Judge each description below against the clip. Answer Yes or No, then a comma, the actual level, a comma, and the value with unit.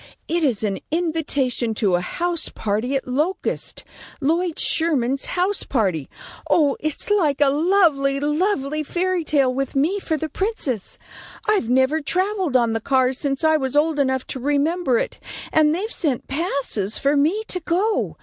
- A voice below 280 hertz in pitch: No, very high, 290 Hz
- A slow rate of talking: No, average, 160 wpm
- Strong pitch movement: No, average, 4.6 semitones